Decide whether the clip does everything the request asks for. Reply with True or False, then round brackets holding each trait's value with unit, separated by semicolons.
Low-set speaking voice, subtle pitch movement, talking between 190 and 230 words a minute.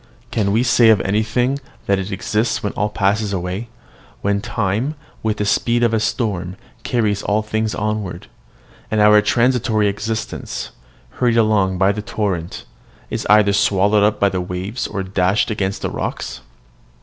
False (105 Hz; 2.1 semitones; 160 wpm)